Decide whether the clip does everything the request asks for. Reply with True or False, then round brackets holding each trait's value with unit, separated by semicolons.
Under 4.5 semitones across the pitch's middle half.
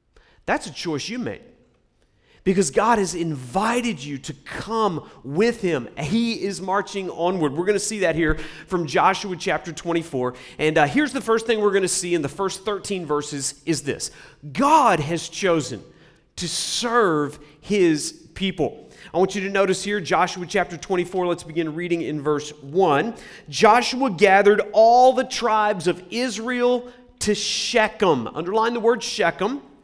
False (5.2 semitones)